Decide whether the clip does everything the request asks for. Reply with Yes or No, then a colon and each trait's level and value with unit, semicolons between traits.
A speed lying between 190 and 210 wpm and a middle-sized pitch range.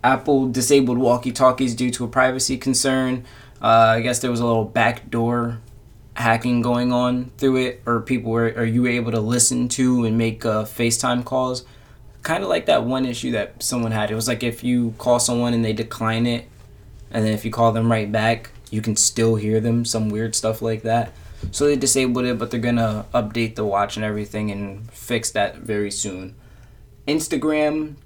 No: average, 200 wpm; narrow, 1.8 semitones